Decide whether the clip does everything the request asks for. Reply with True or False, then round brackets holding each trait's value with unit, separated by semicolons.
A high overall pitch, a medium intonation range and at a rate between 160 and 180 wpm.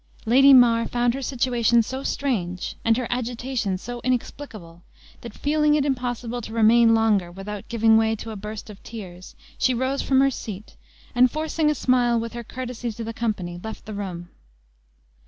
True (235 Hz; 3.0 semitones; 175 wpm)